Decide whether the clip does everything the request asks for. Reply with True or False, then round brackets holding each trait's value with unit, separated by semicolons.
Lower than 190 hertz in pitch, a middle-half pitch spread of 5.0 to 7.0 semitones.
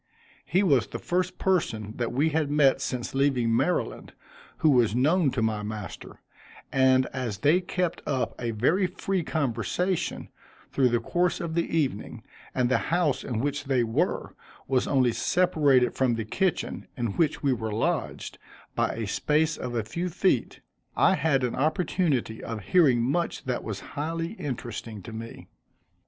True (135 Hz; 5.6 semitones)